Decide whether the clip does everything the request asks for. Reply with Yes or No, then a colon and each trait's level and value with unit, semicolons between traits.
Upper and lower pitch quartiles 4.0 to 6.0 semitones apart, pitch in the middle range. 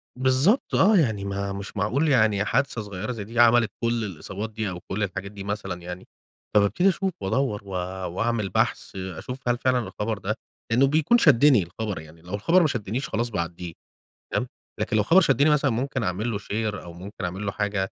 No: average, 4.4 semitones; low, 110 Hz